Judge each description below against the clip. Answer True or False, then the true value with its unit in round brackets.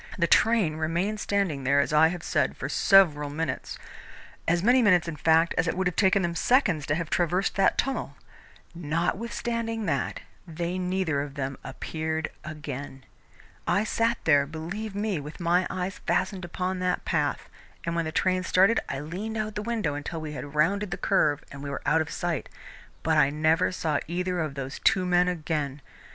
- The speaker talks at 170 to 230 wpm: True (190 wpm)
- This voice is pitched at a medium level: True (170 Hz)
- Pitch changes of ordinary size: True (3.9 semitones)